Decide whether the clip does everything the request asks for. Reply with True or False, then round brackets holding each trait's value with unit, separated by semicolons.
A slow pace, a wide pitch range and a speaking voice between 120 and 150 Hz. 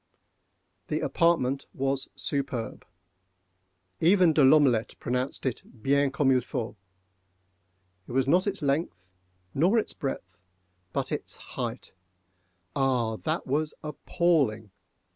True (105 wpm; 5.9 semitones; 135 Hz)